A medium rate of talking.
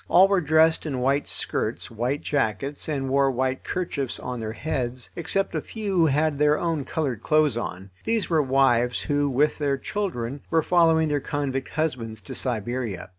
Yes: average, 180 wpm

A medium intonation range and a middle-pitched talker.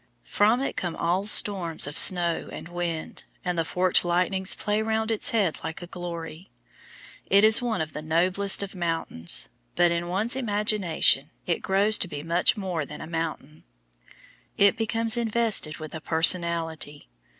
Yes: average, 4.0 semitones; medium, 175 Hz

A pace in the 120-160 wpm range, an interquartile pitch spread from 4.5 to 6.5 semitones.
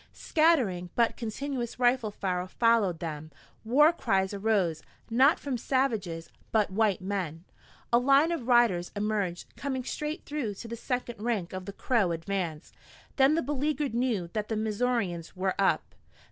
Yes: average, 150 wpm; wide, 5.4 semitones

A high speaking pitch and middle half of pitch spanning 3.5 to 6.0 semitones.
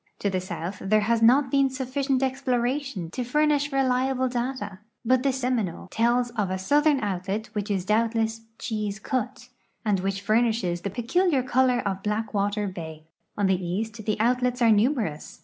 Yes: high, 230 Hz; average, 4.2 semitones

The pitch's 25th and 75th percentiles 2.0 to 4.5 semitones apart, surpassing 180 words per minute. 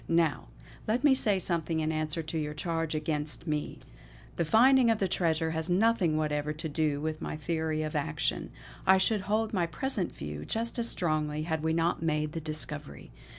Yes: average, 3.6 semitones; average, 190 wpm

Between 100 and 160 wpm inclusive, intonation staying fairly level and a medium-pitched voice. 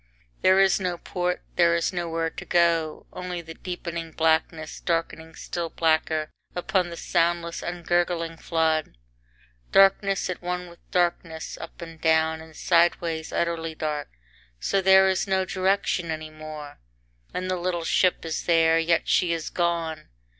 Yes: average, 145 wpm; narrow, 1.8 semitones; medium, 170 Hz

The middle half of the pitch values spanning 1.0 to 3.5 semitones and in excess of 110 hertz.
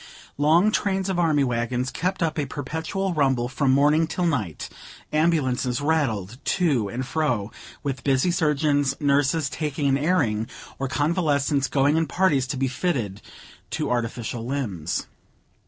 No: average, 4.1 semitones; medium, 140 Hz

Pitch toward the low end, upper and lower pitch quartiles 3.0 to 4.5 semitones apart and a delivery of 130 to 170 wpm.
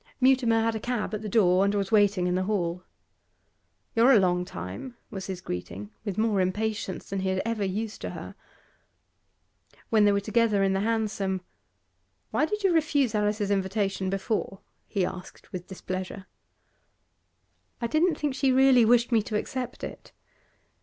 No: high, 210 Hz; average, 3.4 semitones; average, 165 wpm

